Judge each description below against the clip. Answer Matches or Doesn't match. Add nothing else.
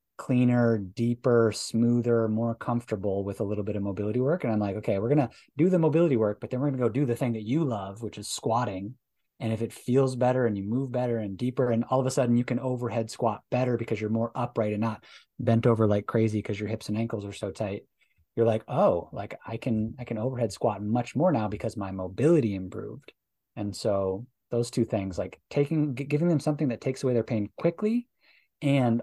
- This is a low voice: Matches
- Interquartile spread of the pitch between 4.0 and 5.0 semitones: Doesn't match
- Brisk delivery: Matches